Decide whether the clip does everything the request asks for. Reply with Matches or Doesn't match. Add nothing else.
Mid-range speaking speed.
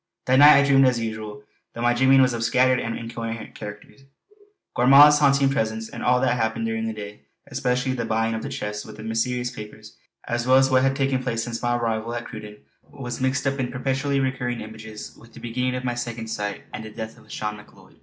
Doesn't match